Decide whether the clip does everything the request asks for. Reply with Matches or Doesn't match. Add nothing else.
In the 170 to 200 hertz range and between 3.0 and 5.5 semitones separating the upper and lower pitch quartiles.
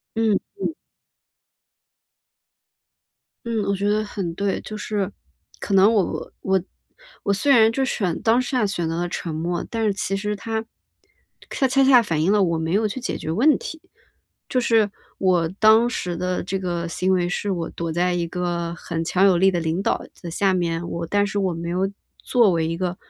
Matches